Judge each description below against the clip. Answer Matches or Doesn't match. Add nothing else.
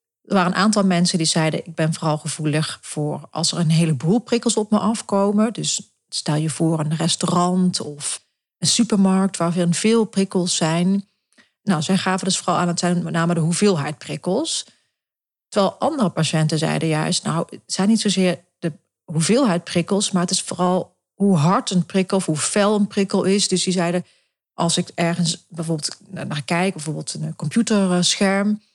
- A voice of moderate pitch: Matches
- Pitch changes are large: Doesn't match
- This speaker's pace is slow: Doesn't match